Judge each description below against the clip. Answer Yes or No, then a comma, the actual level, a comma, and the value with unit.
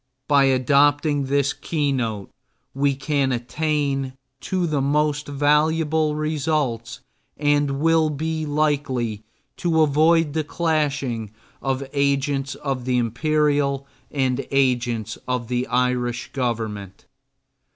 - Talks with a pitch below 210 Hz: Yes, medium, 140 Hz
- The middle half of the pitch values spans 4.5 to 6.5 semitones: No, average, 3.1 semitones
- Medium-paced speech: No, slow, 105 wpm